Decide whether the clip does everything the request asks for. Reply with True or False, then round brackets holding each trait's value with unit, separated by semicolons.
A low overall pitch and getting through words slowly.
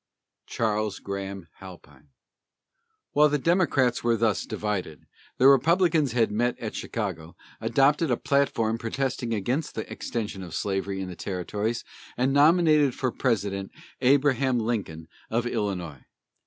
True (115 Hz; 130 wpm)